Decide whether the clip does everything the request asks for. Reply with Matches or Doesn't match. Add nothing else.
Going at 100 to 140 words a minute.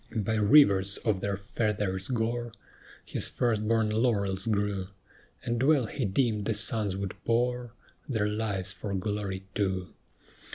Matches